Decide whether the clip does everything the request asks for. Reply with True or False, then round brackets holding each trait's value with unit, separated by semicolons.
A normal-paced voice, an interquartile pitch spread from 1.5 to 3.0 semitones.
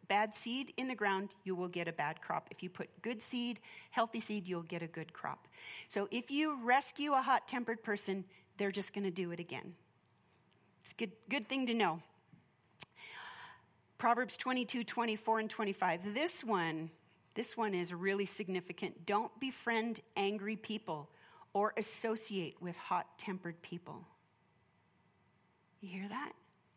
False (155 wpm; 4.2 semitones)